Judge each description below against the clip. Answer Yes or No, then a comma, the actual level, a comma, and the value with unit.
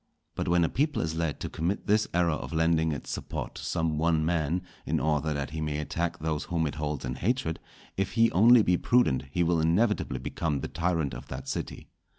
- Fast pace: Yes, fast, 215 wpm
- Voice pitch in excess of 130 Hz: No, very low, 80 Hz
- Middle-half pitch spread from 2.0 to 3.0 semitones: Yes, average, 2.7 semitones